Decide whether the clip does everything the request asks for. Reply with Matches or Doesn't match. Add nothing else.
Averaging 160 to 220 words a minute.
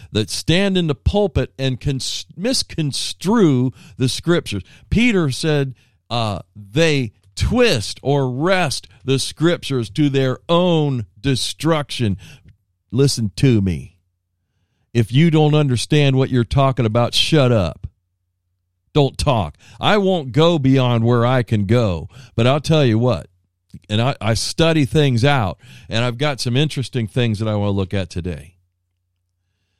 Doesn't match